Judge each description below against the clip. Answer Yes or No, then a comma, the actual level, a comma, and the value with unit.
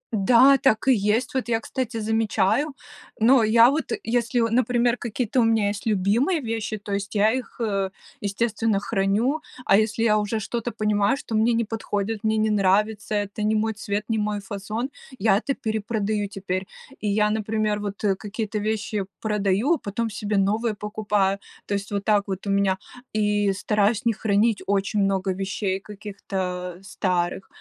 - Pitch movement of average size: No, narrow, 2.0 semitones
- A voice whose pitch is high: Yes, high, 210 Hz